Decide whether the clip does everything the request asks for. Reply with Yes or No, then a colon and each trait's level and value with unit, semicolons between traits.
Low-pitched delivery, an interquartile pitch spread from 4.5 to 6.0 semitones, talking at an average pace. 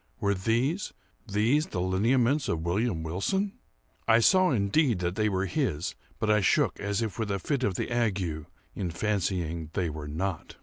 Yes: low, 100 Hz; average, 5.0 semitones; average, 170 wpm